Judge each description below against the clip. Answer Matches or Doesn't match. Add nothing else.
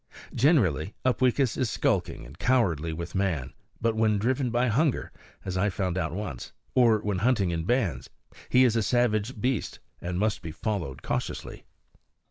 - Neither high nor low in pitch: Doesn't match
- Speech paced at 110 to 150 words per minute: Doesn't match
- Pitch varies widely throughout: Matches